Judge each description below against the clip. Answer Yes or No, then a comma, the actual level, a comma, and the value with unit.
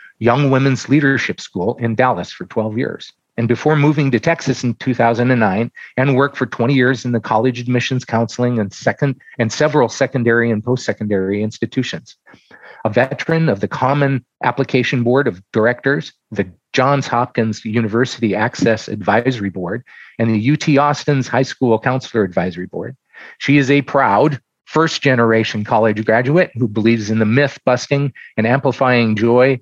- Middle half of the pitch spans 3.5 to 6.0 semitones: No, average, 3.1 semitones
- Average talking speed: Yes, average, 150 wpm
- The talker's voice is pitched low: Yes, low, 125 Hz